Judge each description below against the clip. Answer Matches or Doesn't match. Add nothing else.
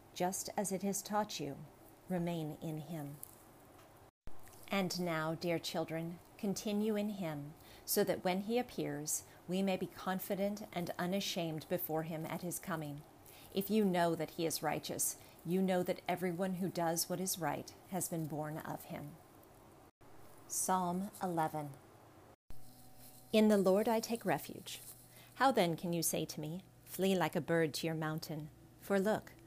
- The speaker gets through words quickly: Doesn't match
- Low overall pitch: Doesn't match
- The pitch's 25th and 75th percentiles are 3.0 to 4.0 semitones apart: Matches